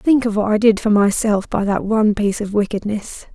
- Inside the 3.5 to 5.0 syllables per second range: No, 5.5 syllables/s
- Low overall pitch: No, high, 210 Hz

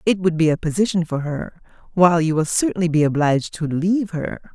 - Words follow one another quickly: Yes, fast, 210 wpm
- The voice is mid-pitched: Yes, medium, 170 Hz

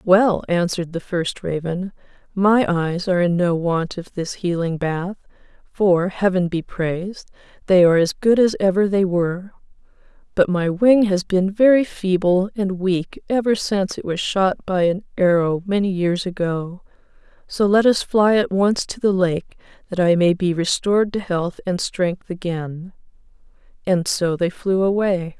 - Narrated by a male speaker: No, female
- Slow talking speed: No, average, 170 wpm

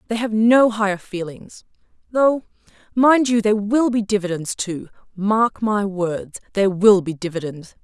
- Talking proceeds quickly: No, average, 155 wpm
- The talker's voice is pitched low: No, high, 205 Hz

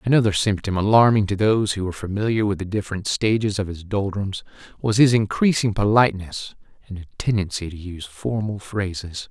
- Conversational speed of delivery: Yes, average, 170 wpm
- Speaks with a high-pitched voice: No, low, 100 Hz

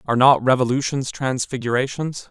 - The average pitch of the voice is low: Yes, low, 130 Hz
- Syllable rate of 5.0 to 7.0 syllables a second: Yes, 5.5 syllables/s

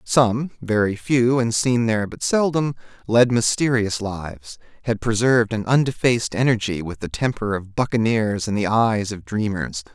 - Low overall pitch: Yes, low, 115 Hz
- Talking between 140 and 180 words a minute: Yes, average, 155 wpm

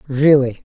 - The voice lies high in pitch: No, low, 135 Hz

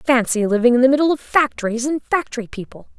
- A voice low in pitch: No, very high, 250 Hz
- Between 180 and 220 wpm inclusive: Yes, average, 200 wpm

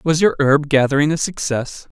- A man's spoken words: Yes, male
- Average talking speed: Yes, average, 180 wpm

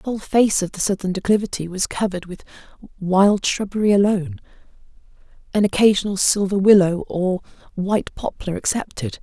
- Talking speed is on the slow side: Yes, slow, 130 wpm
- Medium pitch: No, high, 195 Hz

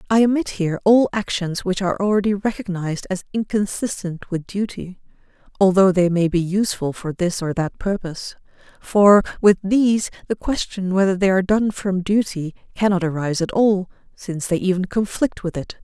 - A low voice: No, high, 190 Hz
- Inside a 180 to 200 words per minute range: No, average, 165 wpm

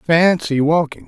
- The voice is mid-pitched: Yes, medium, 160 Hz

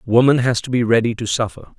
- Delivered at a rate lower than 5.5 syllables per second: No, 5.7 syllables/s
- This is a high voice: No, low, 120 Hz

